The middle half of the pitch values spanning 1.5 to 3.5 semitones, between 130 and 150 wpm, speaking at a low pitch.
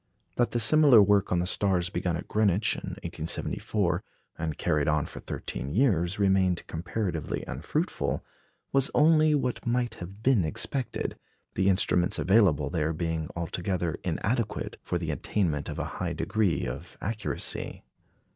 No: average, 5.1 semitones; average, 145 wpm; very low, 95 Hz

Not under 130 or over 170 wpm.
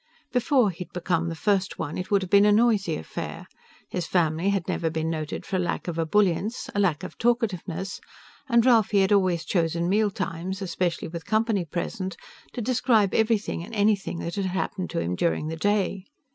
No: average, 185 wpm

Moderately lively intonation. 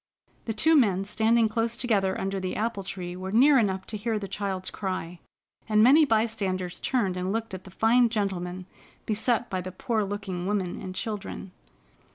Yes: average, 3.2 semitones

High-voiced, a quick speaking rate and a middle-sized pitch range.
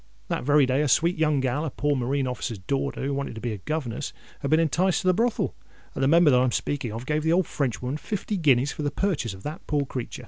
No: medium, 145 Hz; fast, 245 wpm; average, 3.6 semitones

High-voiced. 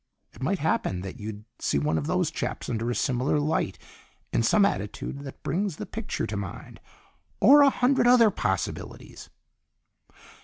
No: low, 135 Hz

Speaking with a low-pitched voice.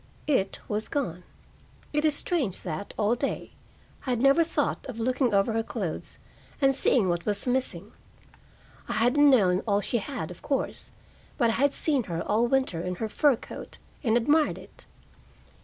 No: high, 235 Hz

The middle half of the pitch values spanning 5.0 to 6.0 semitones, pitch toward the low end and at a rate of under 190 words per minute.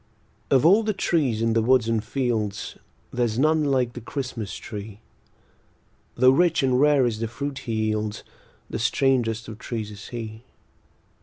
No: average, 3.6 semitones; low, 120 Hz; average, 160 wpm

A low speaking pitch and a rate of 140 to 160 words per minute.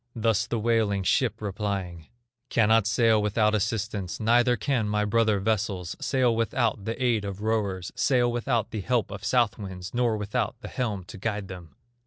No: low, 110 Hz; average, 170 wpm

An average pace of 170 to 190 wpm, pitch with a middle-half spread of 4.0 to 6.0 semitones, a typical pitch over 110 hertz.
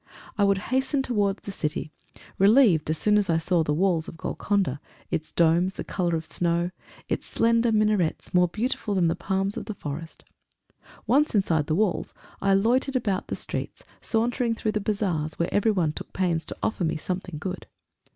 Yes: average, 180 wpm; average, 4.3 semitones; high, 190 Hz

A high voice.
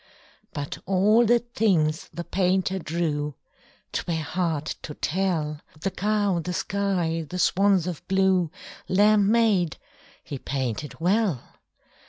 No: medium, 180 Hz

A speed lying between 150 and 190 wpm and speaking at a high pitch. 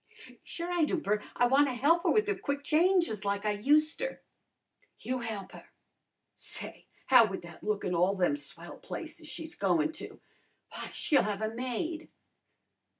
Yes: average, 165 wpm; very high, 255 Hz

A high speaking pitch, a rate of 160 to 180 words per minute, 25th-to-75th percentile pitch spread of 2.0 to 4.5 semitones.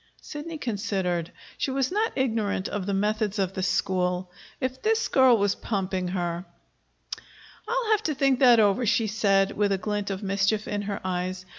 No: high, 205 Hz; average, 175 wpm; average, 5.0 semitones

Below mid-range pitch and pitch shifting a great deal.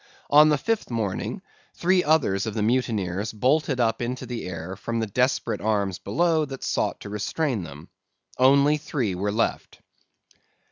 Yes: low, 115 Hz; wide, 5.7 semitones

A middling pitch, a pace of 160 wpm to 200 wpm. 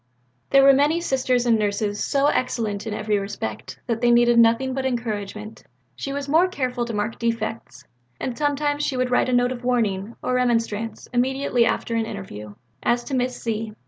No: high, 240 Hz; average, 185 wpm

